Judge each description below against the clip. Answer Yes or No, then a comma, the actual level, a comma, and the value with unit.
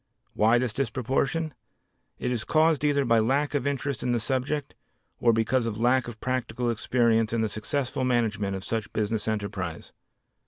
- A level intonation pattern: No, average, 3.2 semitones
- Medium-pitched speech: No, low, 120 Hz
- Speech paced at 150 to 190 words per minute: Yes, average, 165 wpm